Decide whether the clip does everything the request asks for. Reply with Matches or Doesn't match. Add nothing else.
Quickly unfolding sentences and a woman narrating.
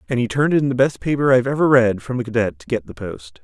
Doesn't match